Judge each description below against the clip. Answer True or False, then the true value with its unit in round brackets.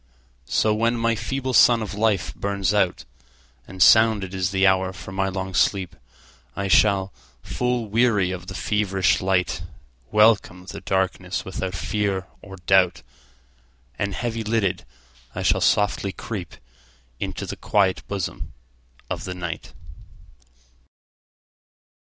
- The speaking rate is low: True (115 wpm)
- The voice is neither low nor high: False (95 Hz)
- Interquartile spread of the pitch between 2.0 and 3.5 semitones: False (4.2 semitones)